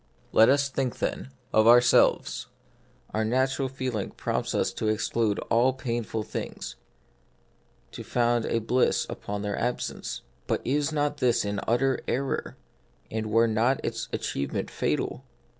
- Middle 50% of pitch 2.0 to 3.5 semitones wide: Yes, average, 3.1 semitones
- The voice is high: No, low, 120 Hz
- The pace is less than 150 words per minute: Yes, average, 140 wpm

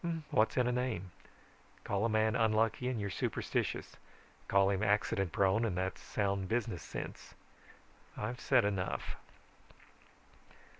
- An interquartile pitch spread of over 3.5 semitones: No, average, 3.0 semitones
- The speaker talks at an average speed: No, slow, 130 wpm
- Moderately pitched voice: No, low, 110 Hz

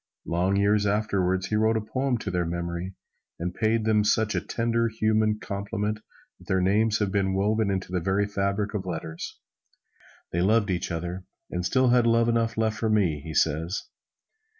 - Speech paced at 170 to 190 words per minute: Yes, average, 180 wpm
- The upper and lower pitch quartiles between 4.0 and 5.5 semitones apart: No, average, 3.2 semitones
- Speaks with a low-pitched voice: Yes, low, 100 Hz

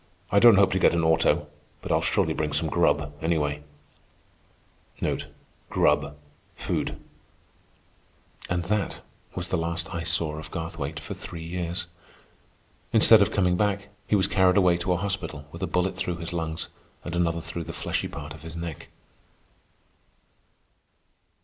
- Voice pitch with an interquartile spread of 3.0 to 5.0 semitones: No, narrow, 2.4 semitones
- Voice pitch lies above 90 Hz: No, very low, 85 Hz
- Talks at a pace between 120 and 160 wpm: Yes, average, 150 wpm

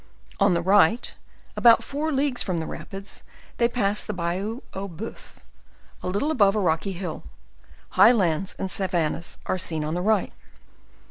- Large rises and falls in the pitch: No, average, 4.2 semitones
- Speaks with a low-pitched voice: No, high, 195 Hz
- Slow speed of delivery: No, average, 160 wpm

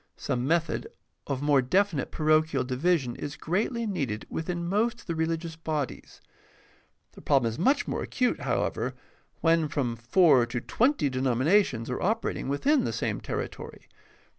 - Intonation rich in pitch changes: Yes, wide, 5.7 semitones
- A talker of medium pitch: Yes, medium, 155 Hz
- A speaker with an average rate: Yes, average, 150 wpm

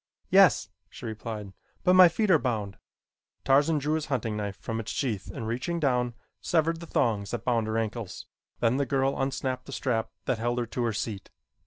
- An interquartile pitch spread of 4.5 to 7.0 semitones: No, average, 4.0 semitones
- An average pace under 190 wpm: No, average, 195 wpm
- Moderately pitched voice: No, low, 120 Hz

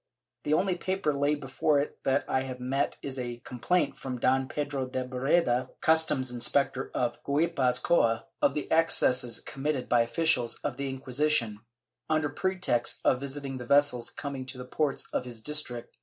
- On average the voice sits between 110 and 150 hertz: Yes, low, 135 Hz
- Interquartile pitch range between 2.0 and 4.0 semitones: Yes, average, 2.9 semitones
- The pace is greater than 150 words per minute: Yes, average, 170 wpm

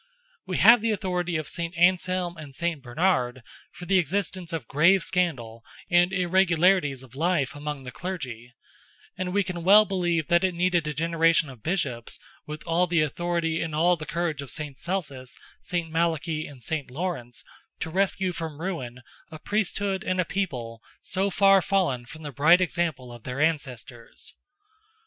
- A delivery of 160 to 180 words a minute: Yes, average, 170 wpm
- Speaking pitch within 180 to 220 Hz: No, medium, 165 Hz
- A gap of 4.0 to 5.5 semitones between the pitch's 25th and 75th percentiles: Yes, average, 4.3 semitones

